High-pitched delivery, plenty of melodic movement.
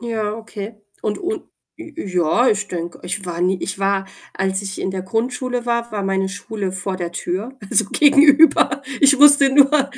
Yes: high, 215 Hz; wide, 5.8 semitones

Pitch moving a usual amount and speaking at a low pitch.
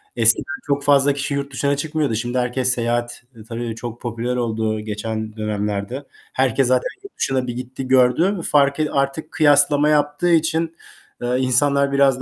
Yes: average, 3.3 semitones; low, 130 Hz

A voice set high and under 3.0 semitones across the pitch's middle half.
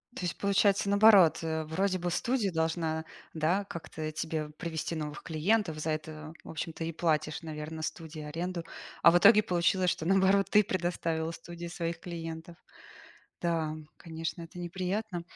No: medium, 170 Hz; narrow, 2.5 semitones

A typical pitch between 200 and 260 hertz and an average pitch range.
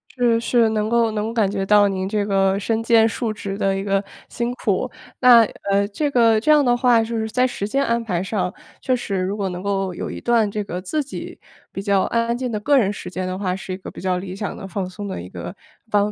Yes: high, 210 Hz; average, 3.1 semitones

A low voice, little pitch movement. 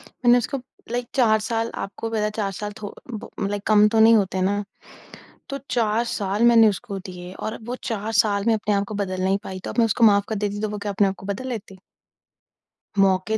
No: high, 210 Hz; narrow, 2.3 semitones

